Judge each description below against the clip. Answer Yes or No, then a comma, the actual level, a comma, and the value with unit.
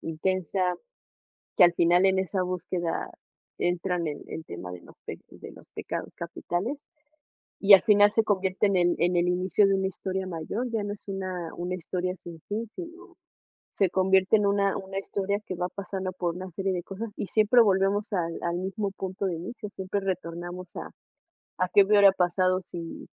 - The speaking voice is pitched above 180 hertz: Yes, high, 190 Hz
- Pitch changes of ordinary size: No, narrow, 2.1 semitones